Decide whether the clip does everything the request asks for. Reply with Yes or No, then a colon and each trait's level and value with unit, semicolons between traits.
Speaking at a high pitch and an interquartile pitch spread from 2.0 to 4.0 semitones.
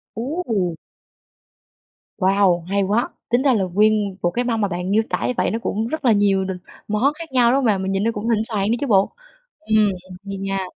Yes: high, 210 Hz; average, 3.3 semitones